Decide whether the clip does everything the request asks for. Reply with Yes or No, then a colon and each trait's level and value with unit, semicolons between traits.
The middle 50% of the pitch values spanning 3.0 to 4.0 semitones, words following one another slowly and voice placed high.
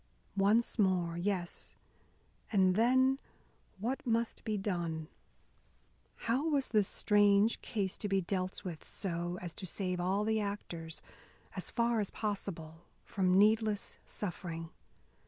Yes: average, 3.6 semitones; slow, 125 wpm; high, 200 Hz